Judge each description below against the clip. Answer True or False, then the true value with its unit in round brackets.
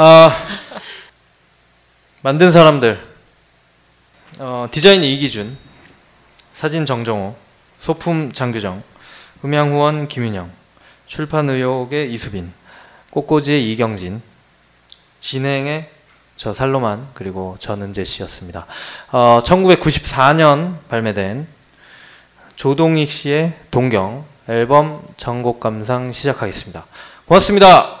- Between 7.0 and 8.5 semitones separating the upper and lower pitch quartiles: False (5.5 semitones)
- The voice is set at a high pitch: False (135 Hz)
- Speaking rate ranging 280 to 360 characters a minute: False (200 characters per minute)